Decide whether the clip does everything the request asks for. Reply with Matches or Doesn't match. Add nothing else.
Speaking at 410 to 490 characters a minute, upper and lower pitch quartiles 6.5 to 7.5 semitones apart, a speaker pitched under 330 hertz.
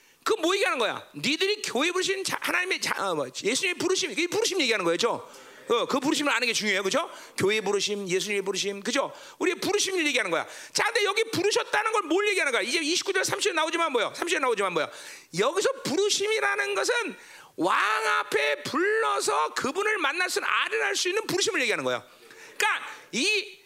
Doesn't match